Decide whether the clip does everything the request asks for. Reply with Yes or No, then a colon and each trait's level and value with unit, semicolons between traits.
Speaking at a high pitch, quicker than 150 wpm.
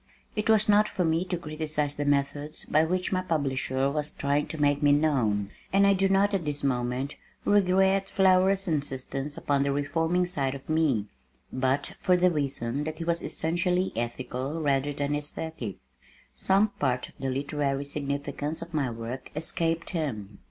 No: medium, 150 Hz; average, 170 wpm